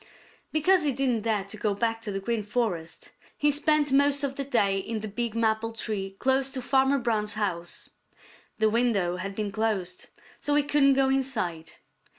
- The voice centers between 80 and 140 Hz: No, high, 225 Hz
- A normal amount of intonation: Yes, average, 5.0 semitones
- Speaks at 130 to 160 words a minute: No, average, 180 wpm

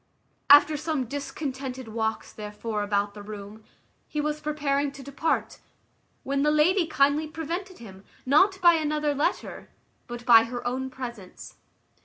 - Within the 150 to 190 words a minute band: No, average, 140 wpm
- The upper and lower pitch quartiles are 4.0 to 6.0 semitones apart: Yes, average, 4.8 semitones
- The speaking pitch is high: Yes, very high, 275 Hz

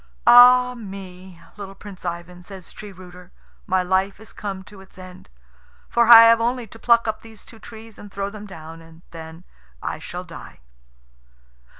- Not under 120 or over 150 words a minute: No, average, 175 wpm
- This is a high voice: Yes, high, 195 Hz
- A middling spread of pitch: Yes, average, 3.7 semitones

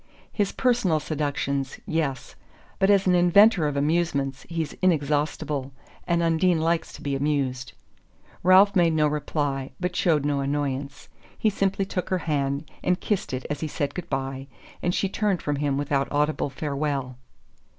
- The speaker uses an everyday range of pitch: Yes, average, 4.1 semitones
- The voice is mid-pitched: Yes, medium, 150 Hz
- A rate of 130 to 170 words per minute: Yes, average, 160 wpm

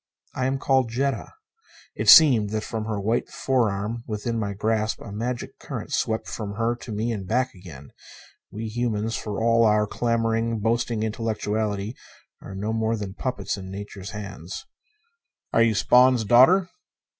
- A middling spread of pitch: No, narrow, 2.2 semitones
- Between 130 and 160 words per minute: Yes, average, 155 wpm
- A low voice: Yes, low, 110 Hz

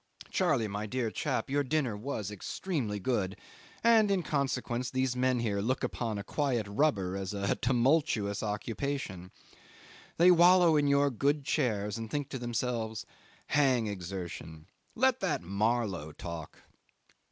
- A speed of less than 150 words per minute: Yes, average, 140 wpm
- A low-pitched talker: Yes, low, 120 Hz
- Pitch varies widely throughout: Yes, wide, 5.8 semitones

